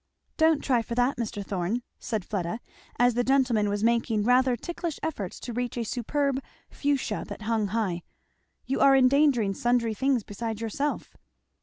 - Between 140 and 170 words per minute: Yes, average, 160 wpm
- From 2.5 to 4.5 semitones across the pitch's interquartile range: Yes, average, 3.8 semitones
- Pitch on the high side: Yes, high, 235 Hz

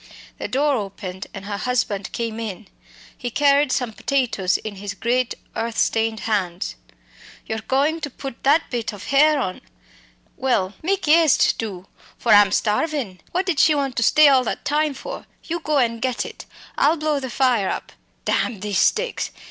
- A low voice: No, high, 245 Hz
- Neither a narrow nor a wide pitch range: No, wide, 5.7 semitones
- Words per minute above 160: Yes, average, 175 wpm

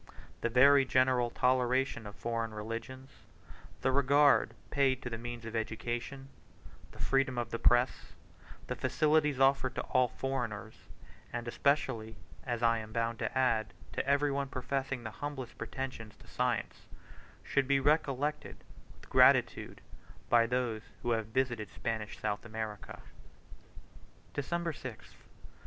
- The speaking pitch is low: Yes, low, 125 Hz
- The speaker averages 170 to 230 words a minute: No, slow, 135 wpm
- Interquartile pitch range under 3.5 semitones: Yes, average, 2.8 semitones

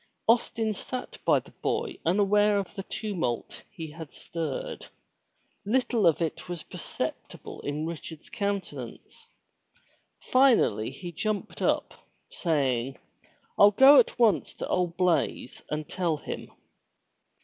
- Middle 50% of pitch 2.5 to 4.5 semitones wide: No, average, 5.1 semitones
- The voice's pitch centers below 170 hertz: No, medium, 185 Hz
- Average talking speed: No, slow, 125 wpm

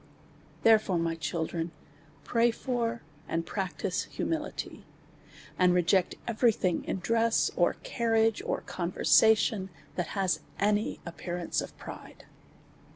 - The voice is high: Yes, high, 195 Hz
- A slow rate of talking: Yes, slow, 115 wpm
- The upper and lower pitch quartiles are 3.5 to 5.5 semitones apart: Yes, average, 4.3 semitones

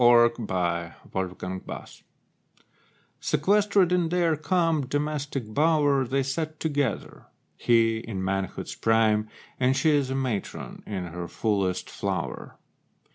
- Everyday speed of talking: No, slow, 110 wpm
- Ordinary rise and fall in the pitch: No, wide, 6.1 semitones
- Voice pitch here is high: No, low, 130 Hz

